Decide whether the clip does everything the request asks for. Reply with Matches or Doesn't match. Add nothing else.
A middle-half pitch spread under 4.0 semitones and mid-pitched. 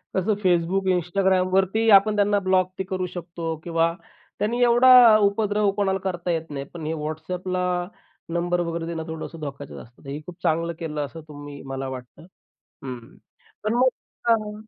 Matches